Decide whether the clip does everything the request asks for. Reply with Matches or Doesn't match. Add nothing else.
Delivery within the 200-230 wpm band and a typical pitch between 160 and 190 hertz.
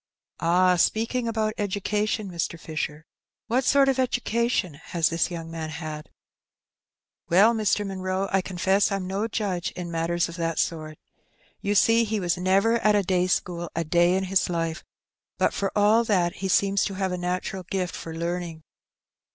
Doesn't match